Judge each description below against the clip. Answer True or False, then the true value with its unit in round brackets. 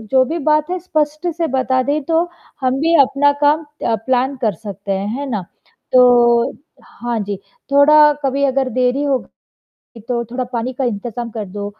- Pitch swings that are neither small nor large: True (3.6 semitones)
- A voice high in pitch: True (260 Hz)